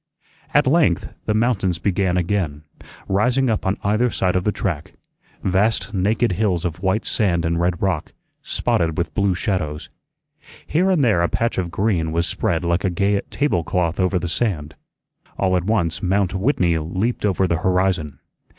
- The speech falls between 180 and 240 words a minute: No, average, 170 wpm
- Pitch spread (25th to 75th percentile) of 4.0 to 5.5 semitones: No, average, 3.3 semitones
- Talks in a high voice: No, very low, 95 Hz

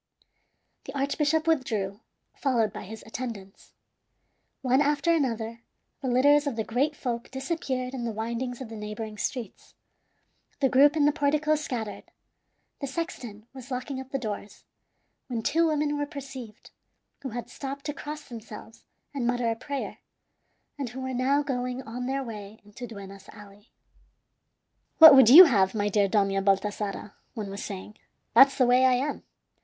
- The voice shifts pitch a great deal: No, average, 4.4 semitones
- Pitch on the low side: No, very high, 250 Hz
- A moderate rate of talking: Yes, average, 160 wpm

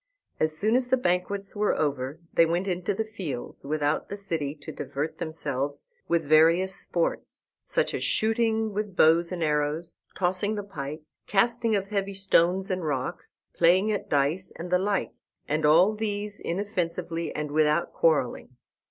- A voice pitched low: No, medium, 175 Hz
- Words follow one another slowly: No, average, 160 wpm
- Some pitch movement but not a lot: Yes, average, 4.6 semitones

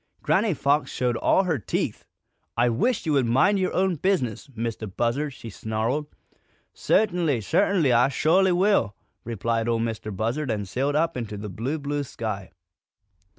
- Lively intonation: Yes, wide, 6.3 semitones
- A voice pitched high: No, low, 130 Hz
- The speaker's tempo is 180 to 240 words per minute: No, average, 155 wpm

